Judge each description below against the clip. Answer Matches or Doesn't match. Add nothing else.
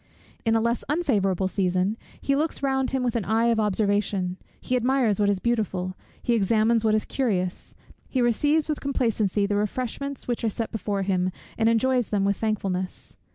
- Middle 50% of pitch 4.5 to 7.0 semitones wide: Doesn't match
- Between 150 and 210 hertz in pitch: Doesn't match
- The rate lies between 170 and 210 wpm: Matches